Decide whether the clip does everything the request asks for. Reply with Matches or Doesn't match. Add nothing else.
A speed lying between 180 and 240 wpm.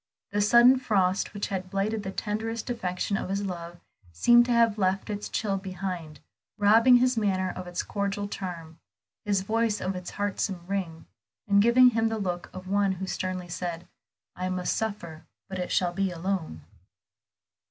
Doesn't match